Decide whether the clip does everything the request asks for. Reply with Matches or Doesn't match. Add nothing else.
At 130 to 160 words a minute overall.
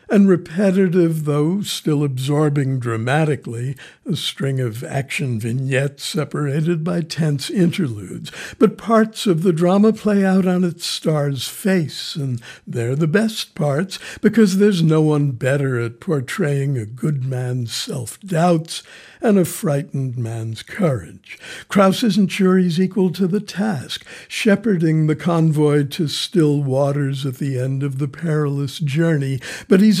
Matches